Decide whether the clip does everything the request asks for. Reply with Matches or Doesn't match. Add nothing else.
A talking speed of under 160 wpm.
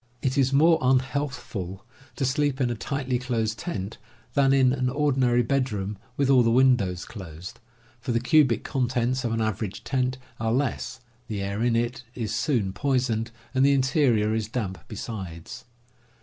Doesn't match